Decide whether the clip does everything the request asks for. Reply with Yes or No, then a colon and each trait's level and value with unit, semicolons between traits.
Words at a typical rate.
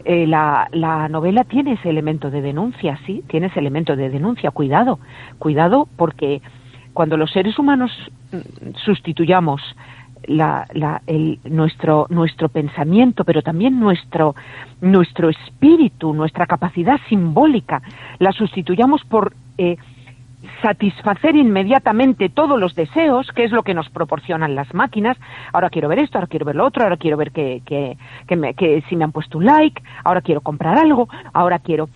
Yes: average, 155 wpm